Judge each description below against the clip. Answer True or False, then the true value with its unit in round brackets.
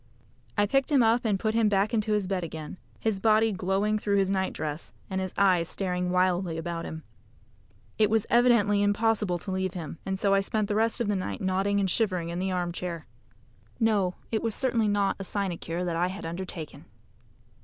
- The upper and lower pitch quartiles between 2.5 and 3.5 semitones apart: True (2.9 semitones)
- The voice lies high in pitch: True (195 Hz)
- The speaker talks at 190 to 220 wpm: True (200 wpm)